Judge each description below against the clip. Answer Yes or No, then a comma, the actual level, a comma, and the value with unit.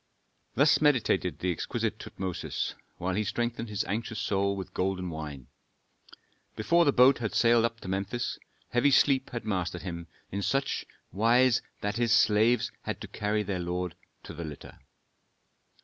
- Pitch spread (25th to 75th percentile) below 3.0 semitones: No, average, 4.5 semitones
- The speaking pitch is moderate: No, low, 105 Hz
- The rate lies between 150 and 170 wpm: Yes, average, 160 wpm